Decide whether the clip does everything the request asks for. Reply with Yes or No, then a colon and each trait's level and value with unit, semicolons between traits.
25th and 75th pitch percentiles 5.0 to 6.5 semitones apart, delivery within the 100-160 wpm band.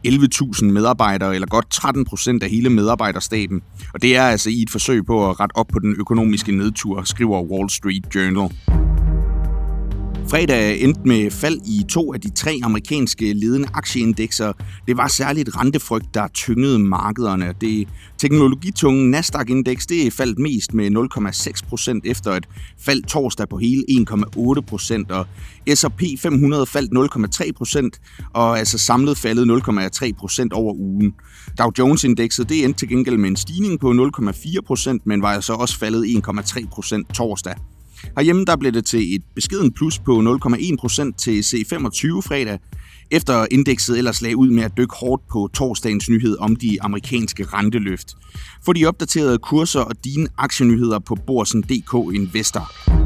No: average, 4.1 semitones; average, 150 wpm